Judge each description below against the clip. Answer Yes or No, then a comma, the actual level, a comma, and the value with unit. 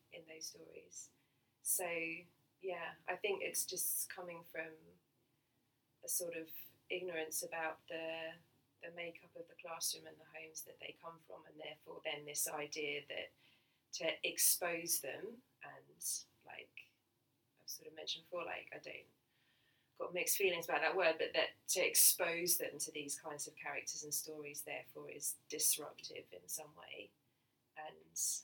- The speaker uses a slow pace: No, average, 155 wpm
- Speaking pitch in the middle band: Yes, medium, 160 Hz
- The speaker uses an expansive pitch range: No, average, 2.8 semitones